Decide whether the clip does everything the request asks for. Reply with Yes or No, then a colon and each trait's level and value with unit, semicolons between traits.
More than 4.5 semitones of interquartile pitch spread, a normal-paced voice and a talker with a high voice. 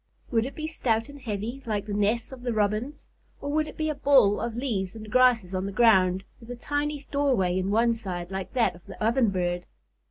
No: average, 5.0 semitones; fast, 220 wpm; high, 225 Hz